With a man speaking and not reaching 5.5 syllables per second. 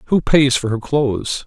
Yes: male; 4.8 syllables/s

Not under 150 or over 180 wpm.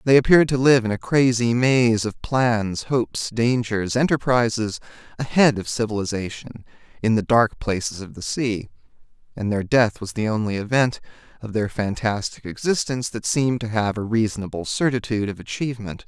Yes: average, 160 wpm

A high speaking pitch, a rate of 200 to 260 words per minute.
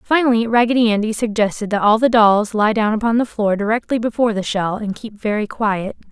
Yes: high, 220 Hz; fast, 205 wpm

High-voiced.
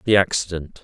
No: very low, 90 Hz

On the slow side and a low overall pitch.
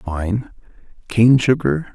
Yes: slow, 90 wpm; low, 110 Hz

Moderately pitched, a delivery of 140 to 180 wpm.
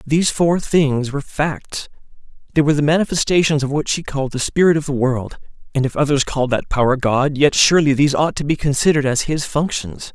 No: medium, 145 Hz; average, 195 wpm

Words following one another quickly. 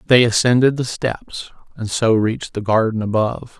No: average, 165 wpm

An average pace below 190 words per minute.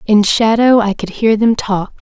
No: average, 200 wpm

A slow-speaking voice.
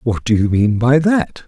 No: fast, 245 wpm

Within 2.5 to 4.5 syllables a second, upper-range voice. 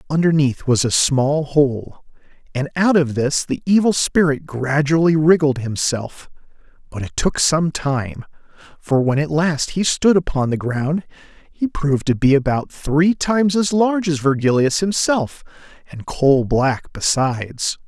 No: 4.2 syllables/s; medium, 150 Hz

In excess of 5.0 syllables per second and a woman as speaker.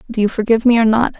Yes: 8.1 syllables/s; female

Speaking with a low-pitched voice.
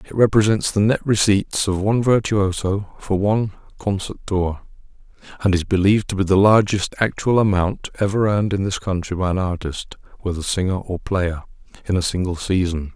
Yes: very low, 95 Hz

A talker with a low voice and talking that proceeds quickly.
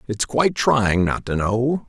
No: low, 115 Hz; average, 190 wpm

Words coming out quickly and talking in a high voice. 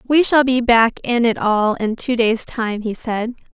Yes: fast, 220 wpm; high, 235 Hz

